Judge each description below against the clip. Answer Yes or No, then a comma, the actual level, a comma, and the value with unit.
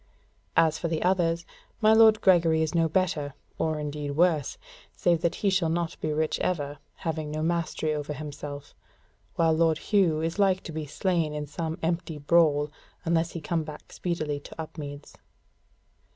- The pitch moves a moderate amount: No, narrow, 2.2 semitones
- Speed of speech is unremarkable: Yes, average, 165 wpm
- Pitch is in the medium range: Yes, medium, 160 Hz